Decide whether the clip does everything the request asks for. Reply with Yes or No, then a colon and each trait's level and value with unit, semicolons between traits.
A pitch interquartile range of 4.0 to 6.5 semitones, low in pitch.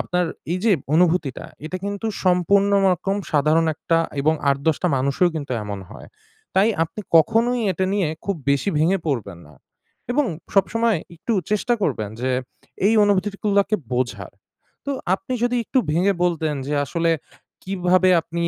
No: average, 4.5 semitones; medium, 180 Hz